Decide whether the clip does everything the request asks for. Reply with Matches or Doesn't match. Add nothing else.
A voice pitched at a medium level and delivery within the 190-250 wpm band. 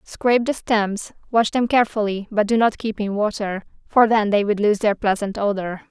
Doesn't match